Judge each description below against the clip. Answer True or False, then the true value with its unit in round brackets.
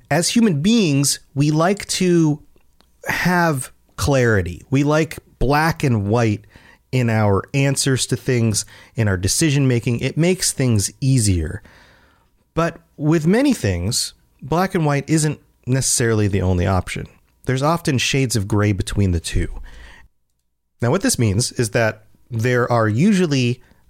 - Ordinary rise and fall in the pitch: False (6.0 semitones)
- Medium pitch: False (125 Hz)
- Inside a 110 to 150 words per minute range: True (140 wpm)